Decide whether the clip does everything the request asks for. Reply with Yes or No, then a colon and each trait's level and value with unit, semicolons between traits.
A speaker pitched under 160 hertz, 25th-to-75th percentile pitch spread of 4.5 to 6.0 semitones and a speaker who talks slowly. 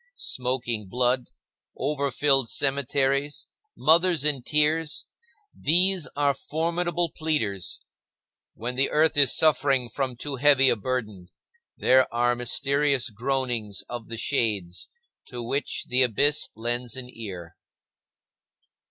No: low, 135 Hz; average, 3.5 semitones; slow, 110 wpm